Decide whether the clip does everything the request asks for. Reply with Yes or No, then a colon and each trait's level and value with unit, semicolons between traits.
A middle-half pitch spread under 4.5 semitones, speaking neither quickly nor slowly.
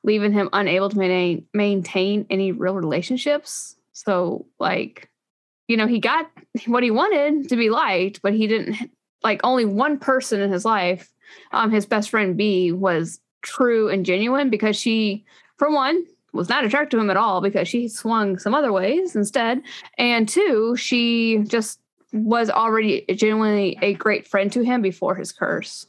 Yes: average, 3.7 semitones; average, 170 wpm